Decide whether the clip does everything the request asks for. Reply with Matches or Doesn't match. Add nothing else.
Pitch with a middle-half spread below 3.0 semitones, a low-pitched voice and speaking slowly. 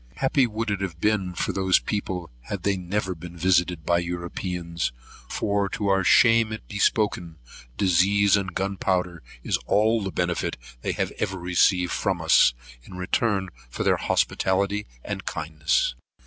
Doesn't match